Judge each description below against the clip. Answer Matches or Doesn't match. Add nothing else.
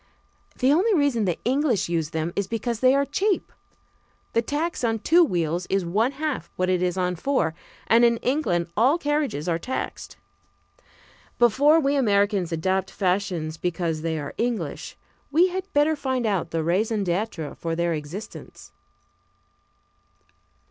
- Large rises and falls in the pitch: Matches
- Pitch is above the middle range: Matches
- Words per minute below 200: Matches